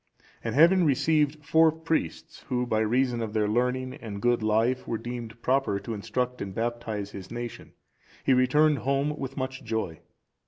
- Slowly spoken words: No, average, 170 wpm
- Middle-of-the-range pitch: No, low, 125 Hz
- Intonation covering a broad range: No, average, 3.6 semitones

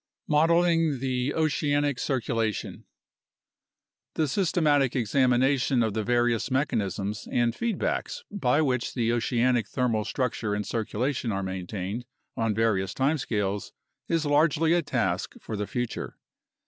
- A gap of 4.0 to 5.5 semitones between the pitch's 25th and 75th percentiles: Yes, average, 4.7 semitones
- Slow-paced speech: Yes, slow, 120 wpm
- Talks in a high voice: No, low, 125 Hz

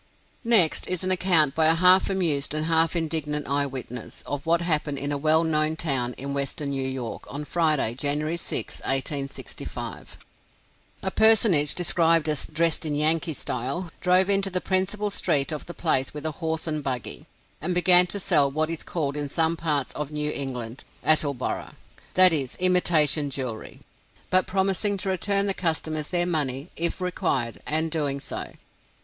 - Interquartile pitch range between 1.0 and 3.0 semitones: No, average, 3.8 semitones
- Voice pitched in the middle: Yes, medium, 155 Hz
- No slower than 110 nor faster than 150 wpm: No, average, 170 wpm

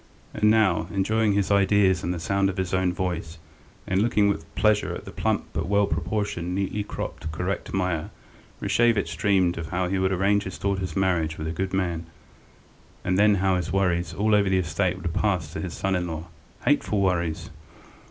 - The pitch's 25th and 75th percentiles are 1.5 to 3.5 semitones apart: Yes, narrow, 2.6 semitones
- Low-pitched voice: Yes, very low, 95 Hz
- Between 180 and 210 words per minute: Yes, average, 190 wpm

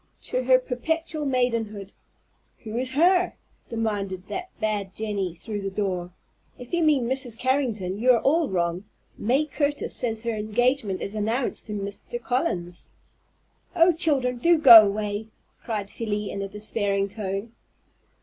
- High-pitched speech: Yes, high, 225 Hz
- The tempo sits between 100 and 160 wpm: Yes, average, 150 wpm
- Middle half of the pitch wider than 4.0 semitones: Yes, average, 4.5 semitones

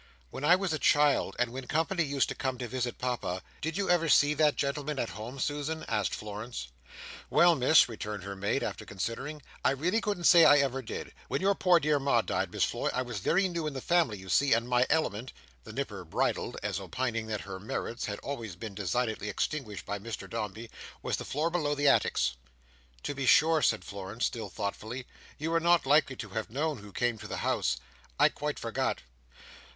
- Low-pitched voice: Yes, low, 130 Hz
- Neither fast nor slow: No, fast, 210 wpm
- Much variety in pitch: Yes, wide, 6.2 semitones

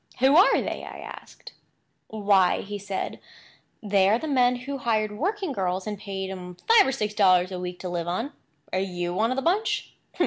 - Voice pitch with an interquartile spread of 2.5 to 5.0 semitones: No, wide, 5.6 semitones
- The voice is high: Yes, high, 210 Hz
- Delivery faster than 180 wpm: Yes, average, 200 wpm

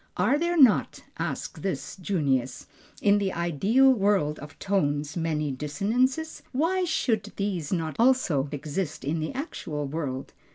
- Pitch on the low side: No, medium, 185 Hz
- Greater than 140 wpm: No, slow, 135 wpm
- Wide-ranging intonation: Yes, wide, 7.9 semitones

